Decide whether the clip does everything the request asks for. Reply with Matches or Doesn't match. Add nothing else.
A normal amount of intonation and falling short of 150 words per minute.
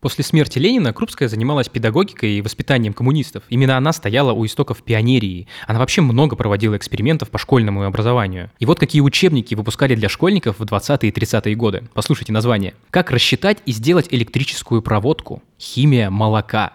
Doesn't match